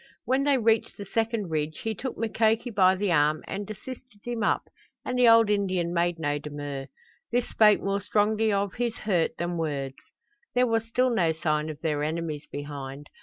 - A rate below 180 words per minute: No, average, 185 wpm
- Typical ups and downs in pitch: No, wide, 6.5 semitones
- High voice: Yes, high, 195 Hz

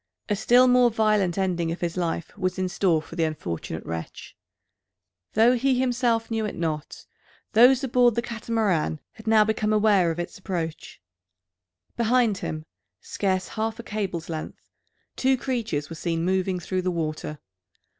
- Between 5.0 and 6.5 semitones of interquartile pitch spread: Yes, average, 5.3 semitones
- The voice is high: Yes, high, 195 Hz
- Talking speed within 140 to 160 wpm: Yes, average, 155 wpm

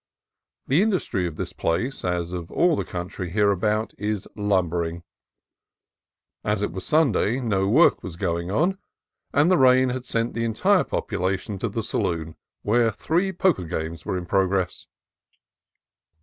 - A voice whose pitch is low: Yes, low, 105 Hz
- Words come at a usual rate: Yes, average, 150 wpm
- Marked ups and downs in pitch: Yes, wide, 6.1 semitones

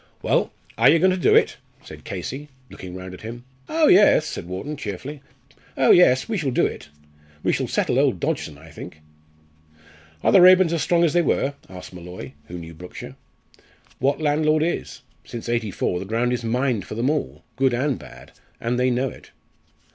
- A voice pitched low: Yes, low, 125 Hz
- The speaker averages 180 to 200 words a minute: Yes, average, 190 wpm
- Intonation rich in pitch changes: Yes, wide, 8.2 semitones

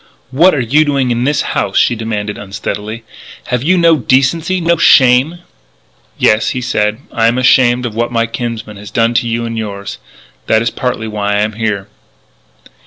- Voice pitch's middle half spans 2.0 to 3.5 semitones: Yes, average, 3.2 semitones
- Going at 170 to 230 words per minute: Yes, average, 180 wpm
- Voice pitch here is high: No, low, 115 Hz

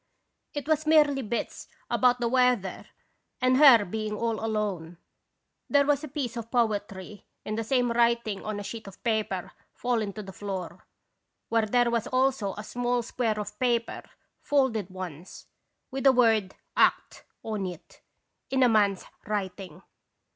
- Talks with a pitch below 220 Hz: No, high, 225 Hz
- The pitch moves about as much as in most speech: Yes, average, 3.6 semitones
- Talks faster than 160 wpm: No, average, 155 wpm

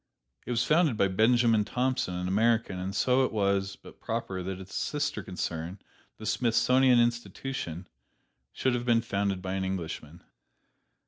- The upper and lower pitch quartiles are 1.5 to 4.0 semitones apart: No, average, 4.4 semitones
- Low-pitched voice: Yes, low, 105 Hz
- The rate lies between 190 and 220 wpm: No, average, 150 wpm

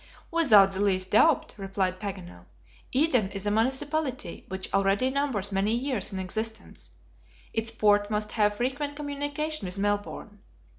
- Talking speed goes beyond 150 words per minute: No, average, 140 wpm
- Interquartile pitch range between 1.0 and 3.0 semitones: No, average, 5.3 semitones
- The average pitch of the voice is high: Yes, high, 210 Hz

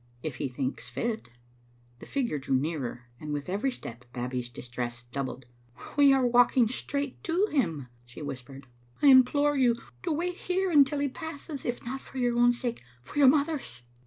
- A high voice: Yes, high, 240 Hz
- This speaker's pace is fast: No, average, 180 wpm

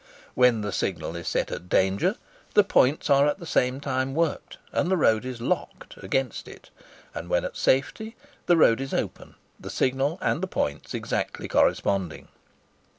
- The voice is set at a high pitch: No, low, 130 Hz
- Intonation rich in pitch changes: Yes, wide, 6.0 semitones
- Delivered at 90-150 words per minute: No, average, 165 wpm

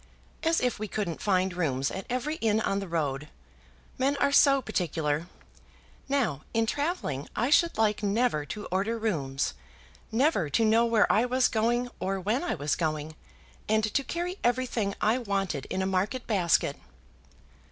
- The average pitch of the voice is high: Yes, high, 215 Hz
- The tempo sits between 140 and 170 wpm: Yes, average, 165 wpm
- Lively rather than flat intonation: Yes, wide, 5.9 semitones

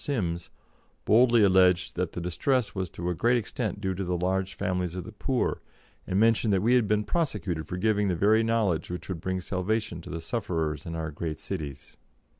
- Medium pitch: No, very low, 95 Hz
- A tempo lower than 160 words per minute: No, fast, 205 wpm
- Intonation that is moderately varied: Yes, average, 4.0 semitones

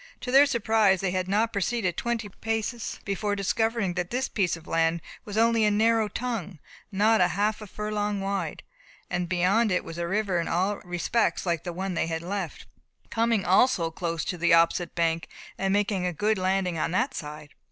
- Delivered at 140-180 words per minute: No, average, 195 wpm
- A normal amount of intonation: Yes, average, 3.7 semitones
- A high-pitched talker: Yes, high, 195 Hz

